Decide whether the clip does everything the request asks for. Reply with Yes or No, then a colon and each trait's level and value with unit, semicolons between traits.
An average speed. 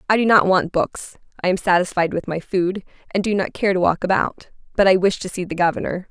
No: fast, 245 wpm